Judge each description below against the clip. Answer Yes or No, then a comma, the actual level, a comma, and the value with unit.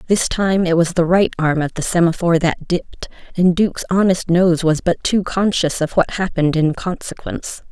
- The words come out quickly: No, average, 185 wpm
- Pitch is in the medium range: Yes, medium, 175 Hz